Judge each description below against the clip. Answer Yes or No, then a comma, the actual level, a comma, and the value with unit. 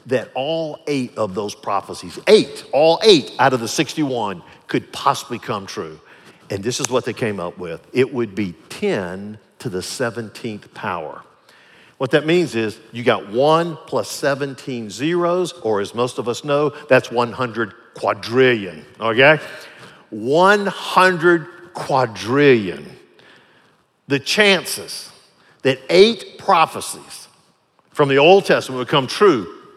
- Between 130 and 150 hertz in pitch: Yes, low, 135 Hz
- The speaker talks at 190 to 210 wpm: No, slow, 135 wpm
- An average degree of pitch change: No, wide, 6.1 semitones